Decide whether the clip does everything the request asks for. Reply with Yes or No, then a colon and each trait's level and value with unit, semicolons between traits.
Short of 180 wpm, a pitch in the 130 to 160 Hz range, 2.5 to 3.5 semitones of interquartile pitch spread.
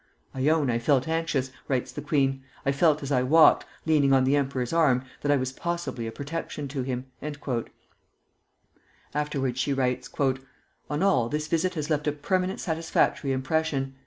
Yes: average, 165 wpm; medium, 140 Hz; average, 3.1 semitones